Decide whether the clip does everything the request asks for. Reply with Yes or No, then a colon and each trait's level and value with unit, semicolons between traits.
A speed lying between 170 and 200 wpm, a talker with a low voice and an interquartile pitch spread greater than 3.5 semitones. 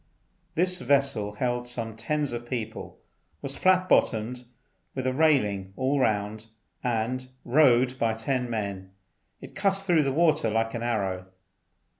No: average, 140 wpm; low, 120 Hz; average, 3.9 semitones